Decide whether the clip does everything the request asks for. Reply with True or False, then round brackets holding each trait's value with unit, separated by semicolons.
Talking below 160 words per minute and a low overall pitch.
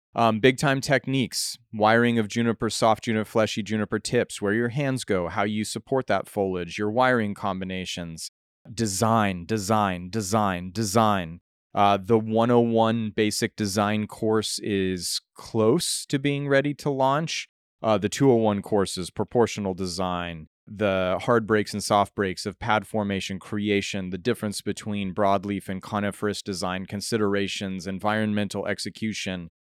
True (135 wpm; 105 Hz)